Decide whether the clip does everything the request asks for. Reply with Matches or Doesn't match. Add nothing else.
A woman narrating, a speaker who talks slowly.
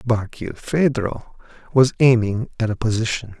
Doesn't match